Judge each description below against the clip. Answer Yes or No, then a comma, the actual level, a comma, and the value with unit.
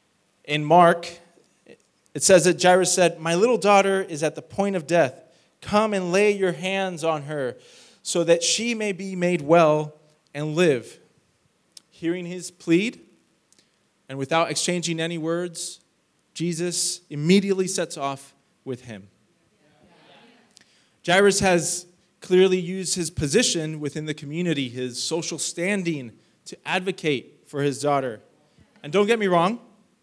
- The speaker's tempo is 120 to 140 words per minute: Yes, slow, 135 wpm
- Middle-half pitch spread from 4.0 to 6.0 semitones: No, average, 3.3 semitones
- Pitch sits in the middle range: Yes, medium, 175 Hz